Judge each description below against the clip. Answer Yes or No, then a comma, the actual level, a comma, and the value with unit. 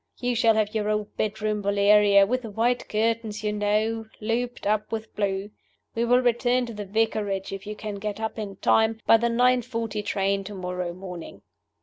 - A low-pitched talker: No, high, 215 Hz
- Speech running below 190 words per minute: No, average, 195 wpm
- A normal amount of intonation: No, narrow, 2.1 semitones